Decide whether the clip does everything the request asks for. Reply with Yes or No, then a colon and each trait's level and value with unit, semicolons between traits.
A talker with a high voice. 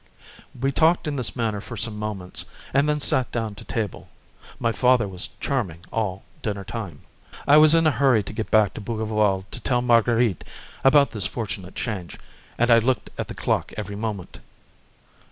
No: low, 115 Hz